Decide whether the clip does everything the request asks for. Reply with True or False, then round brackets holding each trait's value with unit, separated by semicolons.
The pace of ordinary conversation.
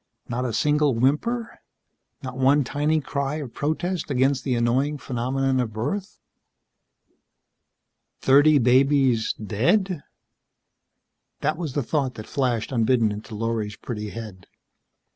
False (120 wpm)